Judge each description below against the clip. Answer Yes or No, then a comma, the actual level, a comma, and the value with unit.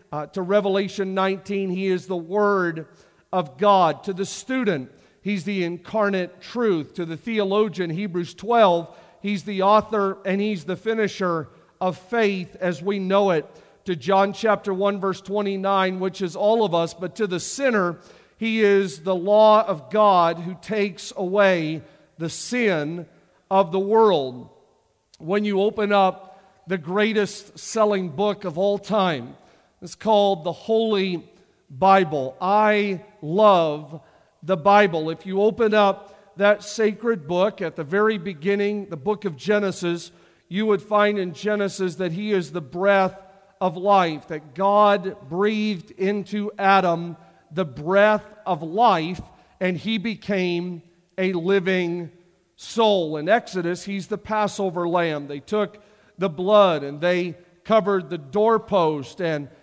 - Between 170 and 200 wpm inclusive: No, average, 145 wpm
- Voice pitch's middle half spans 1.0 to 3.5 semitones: Yes, average, 2.7 semitones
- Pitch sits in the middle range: No, high, 195 Hz